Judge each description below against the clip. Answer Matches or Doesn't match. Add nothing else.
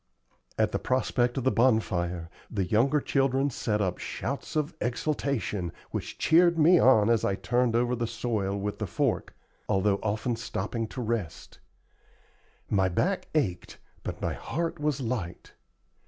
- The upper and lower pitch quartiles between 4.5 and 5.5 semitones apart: Matches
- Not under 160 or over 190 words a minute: Doesn't match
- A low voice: Matches